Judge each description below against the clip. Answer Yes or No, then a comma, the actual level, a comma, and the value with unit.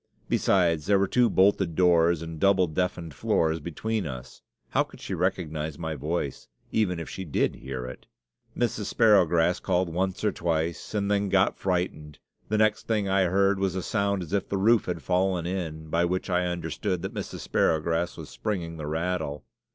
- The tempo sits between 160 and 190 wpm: Yes, average, 180 wpm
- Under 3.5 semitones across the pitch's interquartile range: Yes, average, 3.1 semitones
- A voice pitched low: Yes, very low, 90 Hz